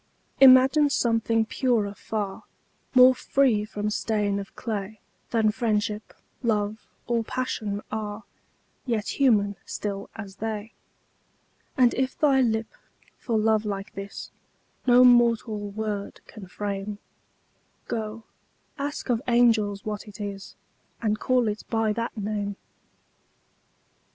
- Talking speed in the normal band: No, slow, 115 wpm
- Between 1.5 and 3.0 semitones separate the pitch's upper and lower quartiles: Yes, narrow, 2.4 semitones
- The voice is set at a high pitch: Yes, high, 220 Hz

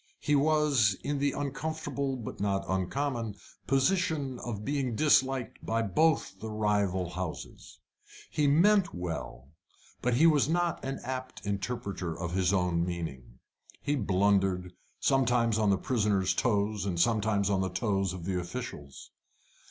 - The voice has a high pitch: No, low, 110 Hz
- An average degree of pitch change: No, wide, 6.4 semitones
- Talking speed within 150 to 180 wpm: No, average, 140 wpm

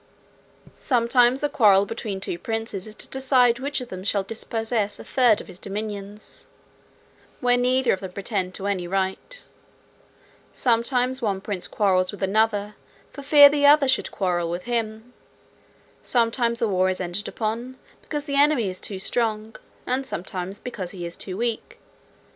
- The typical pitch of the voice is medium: No, high, 220 Hz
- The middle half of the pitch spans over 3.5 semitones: Yes, average, 4.2 semitones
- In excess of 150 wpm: Yes, average, 160 wpm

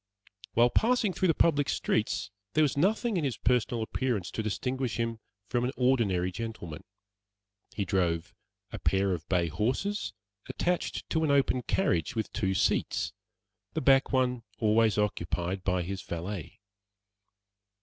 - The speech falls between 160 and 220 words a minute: No, average, 145 wpm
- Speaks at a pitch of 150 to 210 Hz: No, low, 115 Hz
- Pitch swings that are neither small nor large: No, wide, 5.9 semitones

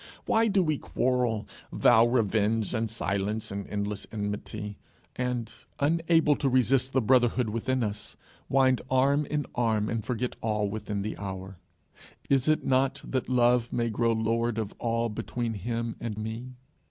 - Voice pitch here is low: Yes, low, 115 Hz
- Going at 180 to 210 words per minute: No, average, 155 wpm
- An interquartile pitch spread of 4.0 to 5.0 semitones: No, average, 3.2 semitones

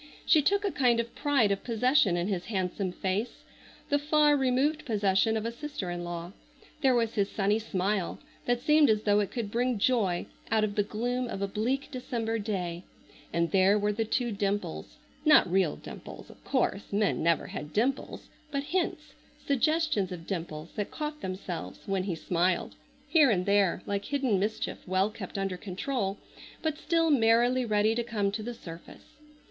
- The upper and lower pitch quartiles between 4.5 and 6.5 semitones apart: Yes, average, 4.9 semitones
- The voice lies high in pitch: Yes, high, 215 Hz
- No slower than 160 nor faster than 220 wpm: Yes, average, 175 wpm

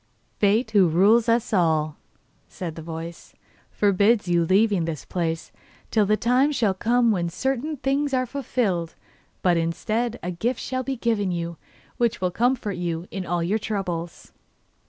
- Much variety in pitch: Yes, wide, 5.7 semitones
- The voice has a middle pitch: No, high, 200 Hz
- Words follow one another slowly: No, average, 155 wpm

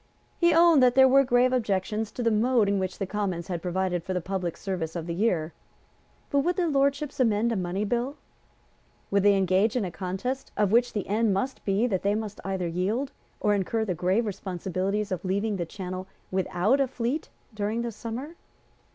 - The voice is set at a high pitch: Yes, high, 205 Hz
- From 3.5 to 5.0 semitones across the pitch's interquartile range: Yes, average, 4.6 semitones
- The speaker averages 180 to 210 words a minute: Yes, average, 200 wpm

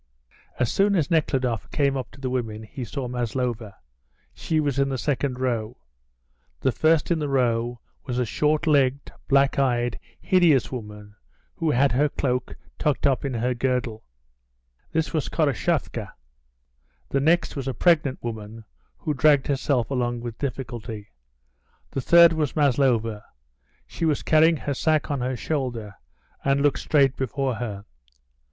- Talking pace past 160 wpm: No, average, 150 wpm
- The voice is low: Yes, low, 130 Hz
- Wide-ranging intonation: No, average, 3.4 semitones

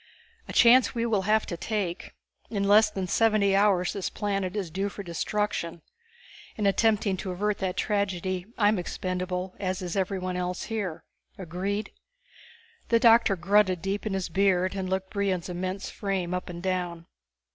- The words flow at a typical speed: Yes, average, 160 wpm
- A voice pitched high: Yes, high, 195 Hz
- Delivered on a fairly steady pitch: Yes, narrow, 2.2 semitones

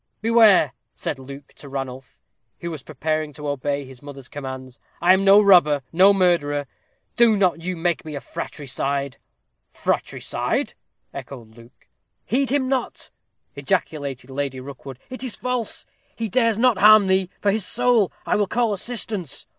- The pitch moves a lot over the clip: Yes, wide, 7.2 semitones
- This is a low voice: No, medium, 165 Hz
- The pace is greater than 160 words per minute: No, average, 155 wpm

